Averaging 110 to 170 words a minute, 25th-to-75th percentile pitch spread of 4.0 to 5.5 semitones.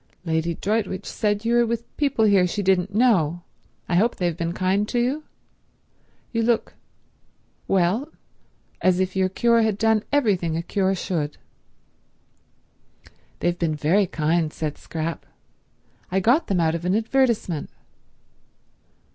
Yes: slow, 135 wpm; average, 4.6 semitones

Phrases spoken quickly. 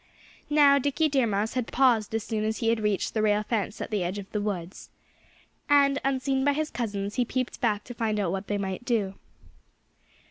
Yes: fast, 210 wpm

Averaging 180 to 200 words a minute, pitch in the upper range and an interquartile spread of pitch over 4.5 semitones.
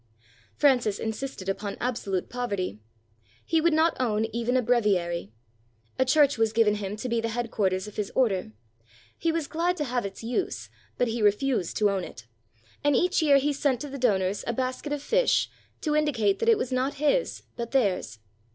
Yes: average, 190 wpm; high, 240 Hz; wide, 5.4 semitones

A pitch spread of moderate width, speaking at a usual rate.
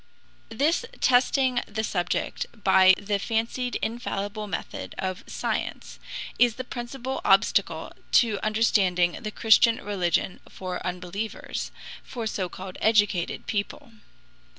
No: average, 3.9 semitones; slow, 110 wpm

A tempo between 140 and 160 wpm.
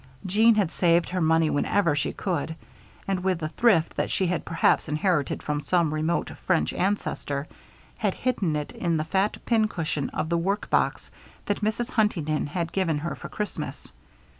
No: average, 170 wpm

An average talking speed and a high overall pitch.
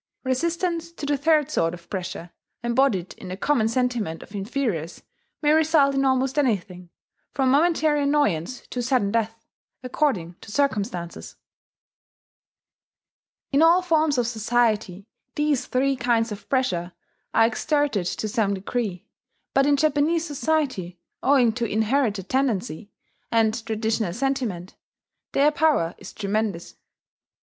No: slow, 125 wpm; high, 245 Hz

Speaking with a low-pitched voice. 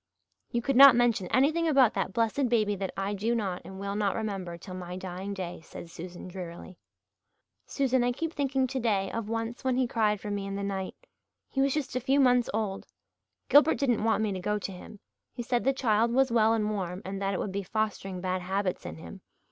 No: high, 210 Hz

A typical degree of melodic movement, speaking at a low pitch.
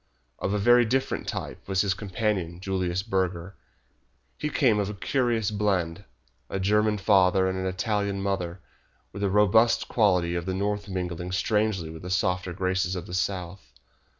No: narrow, 2.3 semitones; very low, 95 Hz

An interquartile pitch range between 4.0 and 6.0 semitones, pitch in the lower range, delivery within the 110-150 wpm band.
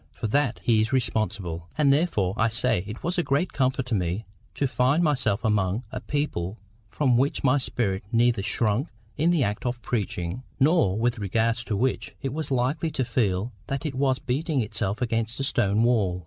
No: average, 4.5 semitones; low, 120 Hz; average, 190 wpm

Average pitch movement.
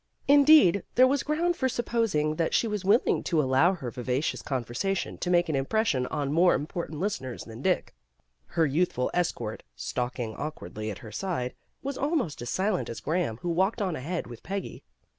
No: wide, 7.5 semitones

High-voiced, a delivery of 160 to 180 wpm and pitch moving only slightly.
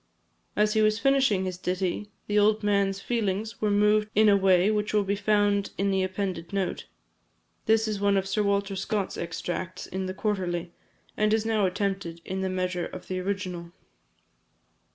Yes: high, 200 Hz; average, 175 wpm; narrow, 2.1 semitones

